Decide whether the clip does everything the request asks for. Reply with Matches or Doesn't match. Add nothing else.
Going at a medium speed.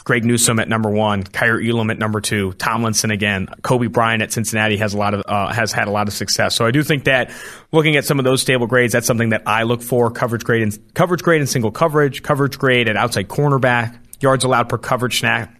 Doesn't match